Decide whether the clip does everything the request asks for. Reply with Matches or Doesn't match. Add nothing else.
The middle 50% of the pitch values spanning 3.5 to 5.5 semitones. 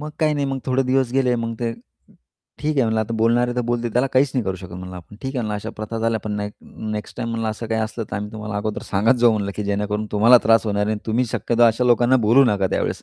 Doesn't match